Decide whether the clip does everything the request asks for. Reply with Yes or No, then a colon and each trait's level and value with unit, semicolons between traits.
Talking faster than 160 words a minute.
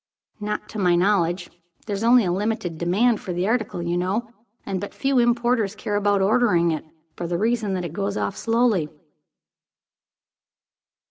Yes: average, 170 wpm